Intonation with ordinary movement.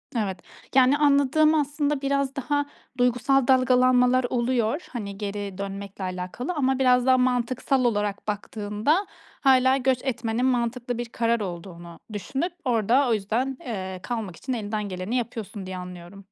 Yes: average, 4.4 semitones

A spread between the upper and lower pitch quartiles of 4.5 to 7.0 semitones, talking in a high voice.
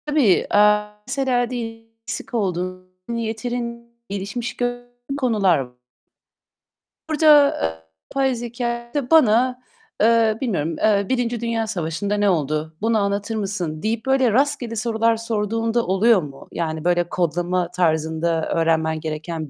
Yes: average, 5.3 semitones; high, 220 Hz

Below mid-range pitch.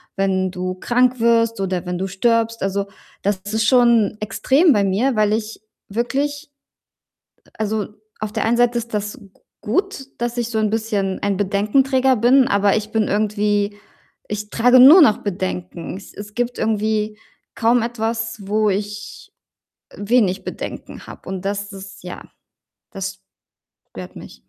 No: high, 215 Hz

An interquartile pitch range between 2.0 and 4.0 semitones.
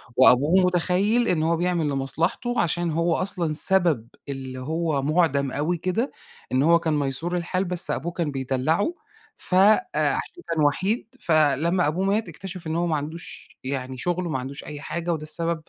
Yes: average, 3.7 semitones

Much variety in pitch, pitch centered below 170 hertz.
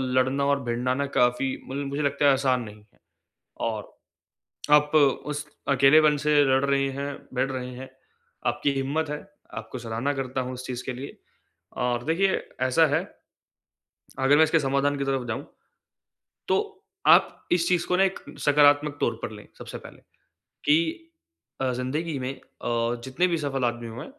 No: narrow, 2.6 semitones; medium, 140 Hz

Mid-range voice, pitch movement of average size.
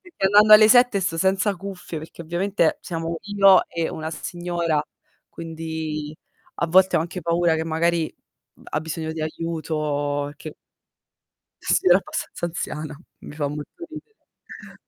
Yes: medium, 165 Hz; average, 3.2 semitones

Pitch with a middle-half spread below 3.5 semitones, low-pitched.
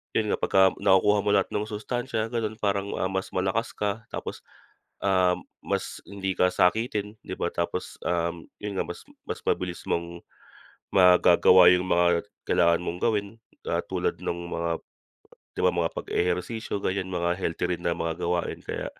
Yes: average, 2.9 semitones; very low, 95 Hz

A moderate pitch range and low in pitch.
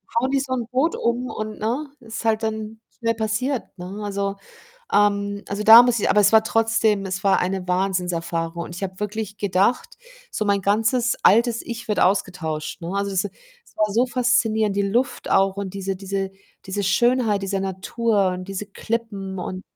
No: average, 3.0 semitones; high, 205 Hz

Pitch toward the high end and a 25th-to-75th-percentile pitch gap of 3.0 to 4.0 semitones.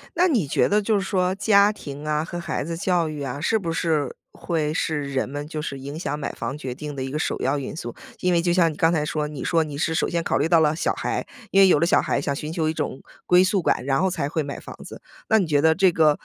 No: medium, 160 Hz; average, 3.3 semitones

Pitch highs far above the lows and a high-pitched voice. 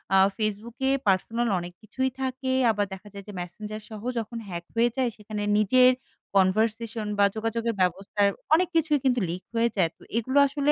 No: average, 3.7 semitones; high, 220 Hz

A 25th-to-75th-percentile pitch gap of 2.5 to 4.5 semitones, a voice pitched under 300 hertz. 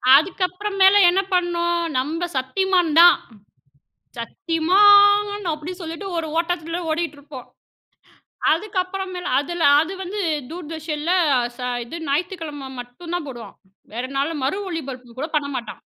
No: average, 4.0 semitones; very high, 335 Hz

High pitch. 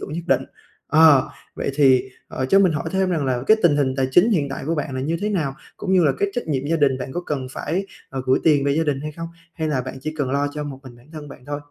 No: medium, 145 Hz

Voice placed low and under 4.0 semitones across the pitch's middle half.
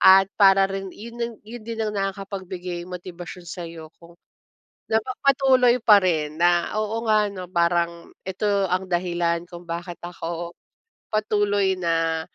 No: medium, 185 Hz; average, 3.5 semitones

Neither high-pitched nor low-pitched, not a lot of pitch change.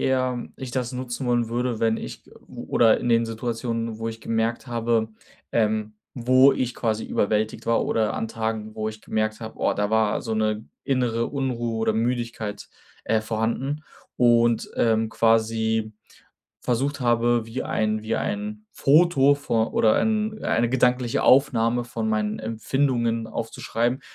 No: low, 115 Hz; narrow, 2.0 semitones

